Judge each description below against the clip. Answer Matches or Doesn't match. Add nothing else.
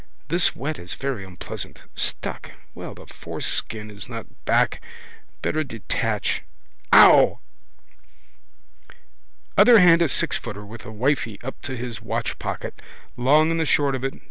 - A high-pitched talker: Doesn't match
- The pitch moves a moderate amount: Doesn't match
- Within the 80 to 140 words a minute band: Matches